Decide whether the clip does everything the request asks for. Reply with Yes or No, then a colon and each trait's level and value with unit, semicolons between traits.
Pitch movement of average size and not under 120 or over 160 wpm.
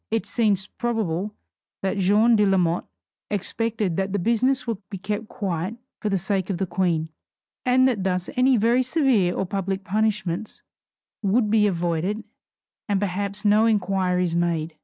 Yes: average, 3.3 semitones; average, 155 wpm